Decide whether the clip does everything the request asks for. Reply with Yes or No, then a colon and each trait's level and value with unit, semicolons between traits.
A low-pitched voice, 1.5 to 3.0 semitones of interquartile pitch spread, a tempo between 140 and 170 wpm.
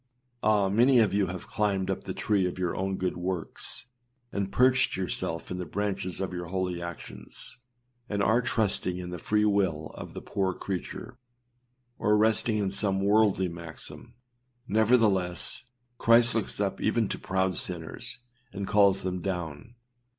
Yes: very low, 95 Hz; average, 2.7 semitones; average, 160 wpm